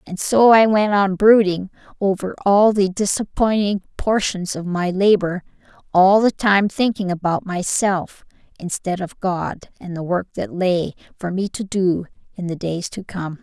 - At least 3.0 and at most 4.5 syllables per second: Yes, 4.2 syllables/s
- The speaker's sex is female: Yes, female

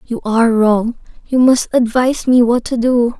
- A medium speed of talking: Yes, average, 190 wpm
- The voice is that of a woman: Yes, female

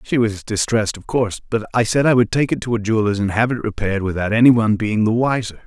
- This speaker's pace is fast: Yes, fast, 265 wpm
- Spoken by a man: Yes, male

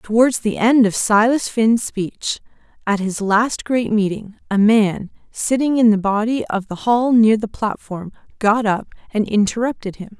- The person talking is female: Yes, female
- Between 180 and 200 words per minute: No, average, 170 wpm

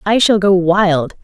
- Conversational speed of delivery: Yes, average, 195 wpm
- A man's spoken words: No, female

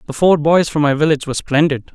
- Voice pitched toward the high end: No, medium, 150 Hz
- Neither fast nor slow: No, fast, 245 wpm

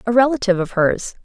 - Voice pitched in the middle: No, high, 215 Hz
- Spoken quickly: No, average, 195 wpm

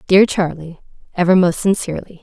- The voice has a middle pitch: Yes, medium, 180 Hz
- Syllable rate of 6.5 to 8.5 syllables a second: No, 5.8 syllables/s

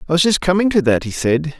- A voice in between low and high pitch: Yes, medium, 160 Hz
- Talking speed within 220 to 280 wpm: No, fast, 300 wpm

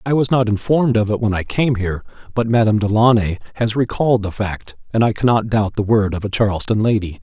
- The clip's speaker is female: No, male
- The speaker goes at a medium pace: No, fast, 225 wpm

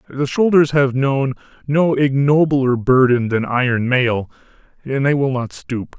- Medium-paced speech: Yes, average, 150 wpm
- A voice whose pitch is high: No, low, 135 Hz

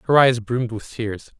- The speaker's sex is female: No, male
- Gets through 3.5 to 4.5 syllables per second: No, 5.0 syllables/s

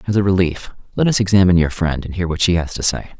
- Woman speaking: No, male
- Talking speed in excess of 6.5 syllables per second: Yes, 6.9 syllables/s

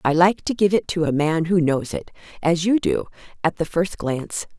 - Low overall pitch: No, medium, 165 Hz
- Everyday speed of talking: No, fast, 235 wpm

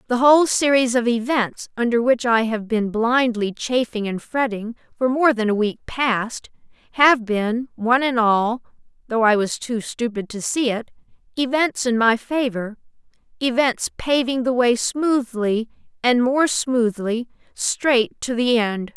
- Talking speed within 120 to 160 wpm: Yes, average, 150 wpm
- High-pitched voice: Yes, high, 240 Hz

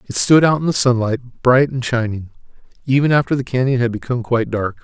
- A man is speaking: Yes, male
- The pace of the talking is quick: Yes, fast, 210 wpm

